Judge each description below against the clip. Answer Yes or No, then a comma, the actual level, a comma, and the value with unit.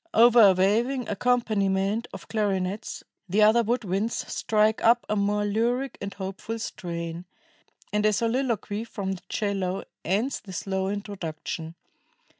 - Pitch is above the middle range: Yes, high, 205 Hz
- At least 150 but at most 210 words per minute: No, slow, 135 wpm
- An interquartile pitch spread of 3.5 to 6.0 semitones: No, average, 3.0 semitones